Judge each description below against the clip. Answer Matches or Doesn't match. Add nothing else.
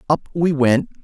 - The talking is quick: Doesn't match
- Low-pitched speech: Doesn't match